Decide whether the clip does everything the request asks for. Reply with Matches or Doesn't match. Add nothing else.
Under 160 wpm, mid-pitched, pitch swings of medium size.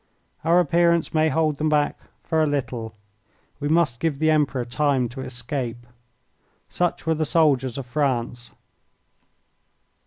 Matches